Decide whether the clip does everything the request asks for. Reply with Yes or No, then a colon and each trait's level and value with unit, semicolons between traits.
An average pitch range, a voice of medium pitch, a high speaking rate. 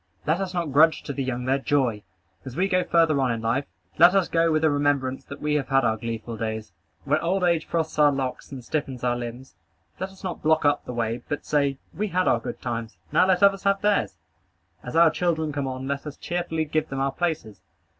Yes: average, 4.5 semitones; medium, 145 Hz; fast, 235 wpm